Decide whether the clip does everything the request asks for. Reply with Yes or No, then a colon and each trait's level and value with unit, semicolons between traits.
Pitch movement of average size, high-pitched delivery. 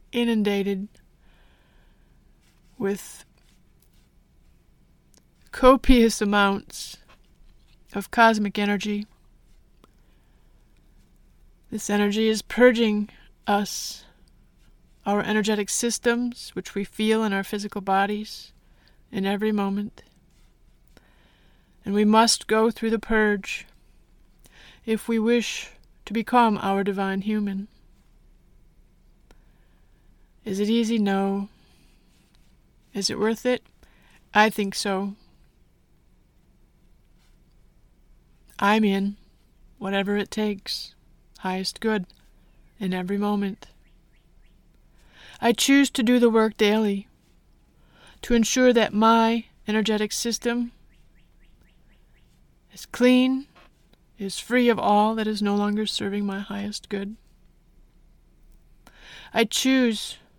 No: narrow, 2.2 semitones; high, 210 Hz